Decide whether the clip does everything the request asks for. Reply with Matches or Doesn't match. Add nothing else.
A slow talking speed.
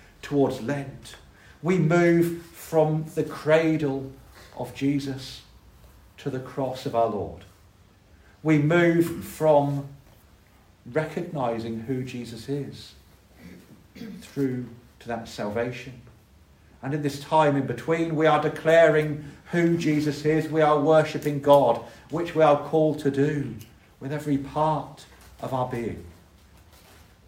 Matches